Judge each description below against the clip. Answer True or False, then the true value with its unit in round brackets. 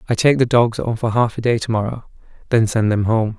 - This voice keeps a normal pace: False (265 wpm)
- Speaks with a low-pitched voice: True (115 Hz)